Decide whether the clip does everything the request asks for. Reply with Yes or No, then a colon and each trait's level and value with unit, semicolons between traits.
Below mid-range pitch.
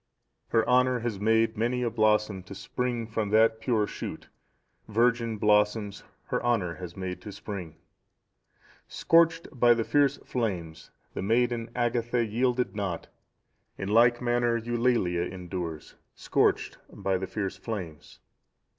Yes: low, 110 Hz